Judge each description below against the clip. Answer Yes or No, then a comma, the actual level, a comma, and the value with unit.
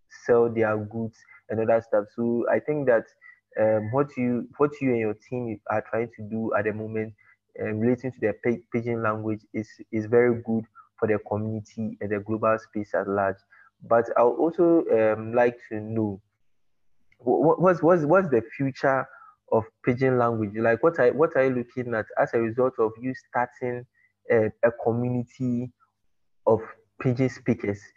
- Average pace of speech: Yes, average, 180 wpm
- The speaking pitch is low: Yes, low, 115 Hz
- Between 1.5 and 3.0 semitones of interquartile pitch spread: Yes, narrow, 2.5 semitones